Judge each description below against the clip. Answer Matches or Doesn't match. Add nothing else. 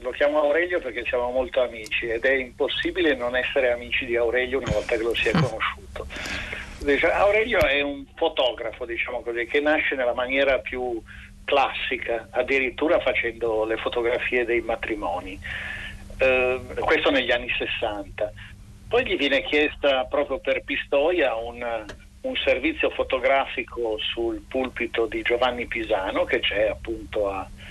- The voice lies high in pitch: Doesn't match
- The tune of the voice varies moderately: Matches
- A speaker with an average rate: Matches